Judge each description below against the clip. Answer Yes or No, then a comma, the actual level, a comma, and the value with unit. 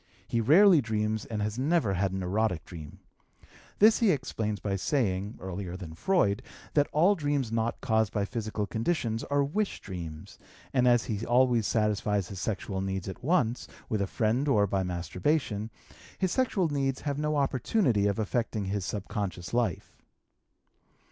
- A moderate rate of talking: Yes, average, 160 wpm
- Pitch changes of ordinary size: No, wide, 5.8 semitones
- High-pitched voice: No, low, 110 Hz